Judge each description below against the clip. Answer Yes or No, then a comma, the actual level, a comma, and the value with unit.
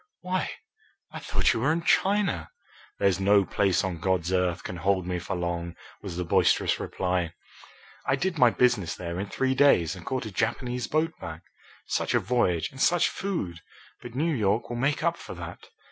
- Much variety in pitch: Yes, wide, 7.1 semitones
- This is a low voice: Yes, low, 100 Hz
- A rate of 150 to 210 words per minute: Yes, average, 190 wpm